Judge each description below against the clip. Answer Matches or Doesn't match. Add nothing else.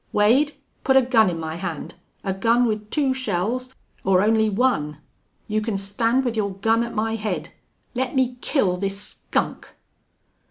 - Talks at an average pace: Matches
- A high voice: Matches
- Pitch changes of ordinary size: Matches